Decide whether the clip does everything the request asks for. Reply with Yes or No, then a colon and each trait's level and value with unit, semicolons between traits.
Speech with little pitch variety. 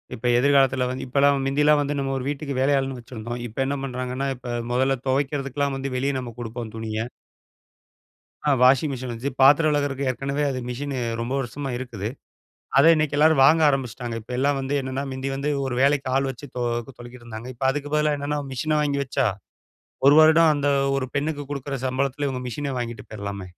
Yes: narrow, 2.3 semitones